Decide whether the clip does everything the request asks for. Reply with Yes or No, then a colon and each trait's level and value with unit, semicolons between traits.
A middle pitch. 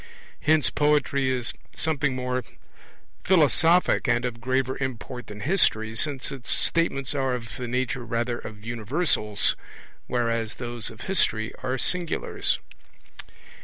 No: low, 125 Hz